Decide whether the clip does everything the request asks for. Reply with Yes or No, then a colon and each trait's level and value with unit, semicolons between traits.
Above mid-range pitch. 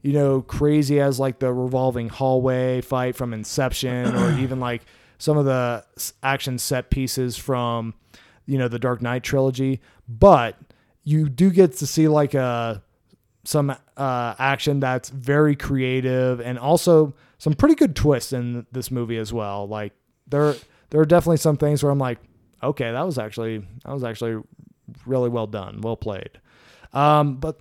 No: low, 130 Hz